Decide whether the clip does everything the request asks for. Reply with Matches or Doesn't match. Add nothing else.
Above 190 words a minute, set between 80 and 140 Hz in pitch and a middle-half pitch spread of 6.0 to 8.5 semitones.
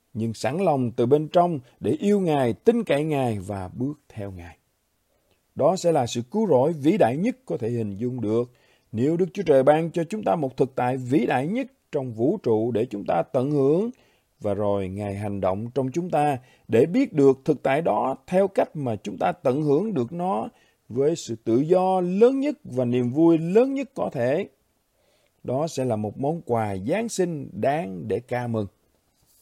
Matches